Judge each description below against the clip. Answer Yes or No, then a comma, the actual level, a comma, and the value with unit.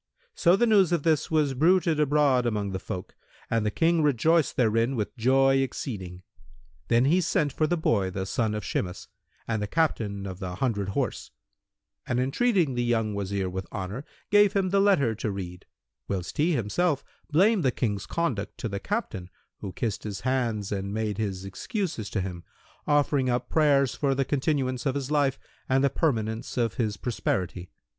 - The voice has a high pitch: No, low, 125 Hz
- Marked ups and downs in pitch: Yes, wide, 6.7 semitones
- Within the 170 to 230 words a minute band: Yes, average, 180 wpm